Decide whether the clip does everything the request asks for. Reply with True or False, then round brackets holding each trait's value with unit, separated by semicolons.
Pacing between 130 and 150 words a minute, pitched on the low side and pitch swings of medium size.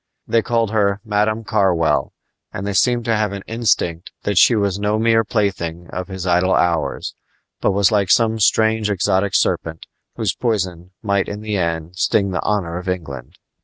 False (175 wpm; 100 Hz; 3.4 semitones)